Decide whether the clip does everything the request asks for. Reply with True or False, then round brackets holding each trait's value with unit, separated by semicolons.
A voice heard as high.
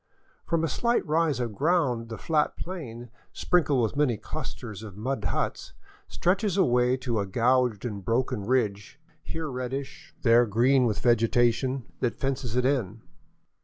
False (125 Hz)